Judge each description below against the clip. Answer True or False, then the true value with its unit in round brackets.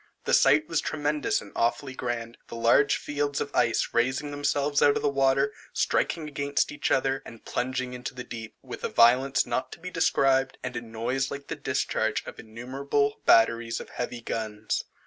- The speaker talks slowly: False (185 wpm)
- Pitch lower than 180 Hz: True (135 Hz)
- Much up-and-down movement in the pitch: False (3.2 semitones)